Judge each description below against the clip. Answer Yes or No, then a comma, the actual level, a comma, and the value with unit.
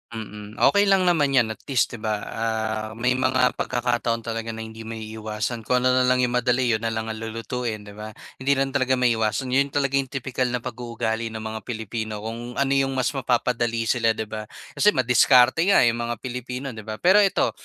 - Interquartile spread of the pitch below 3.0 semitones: Yes, narrow, 2.6 semitones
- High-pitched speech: No, low, 120 Hz